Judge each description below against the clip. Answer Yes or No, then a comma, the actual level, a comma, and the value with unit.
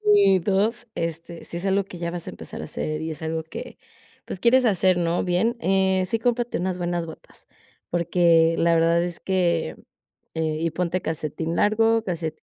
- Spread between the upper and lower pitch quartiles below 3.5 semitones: Yes, narrow, 2.6 semitones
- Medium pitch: Yes, medium, 175 Hz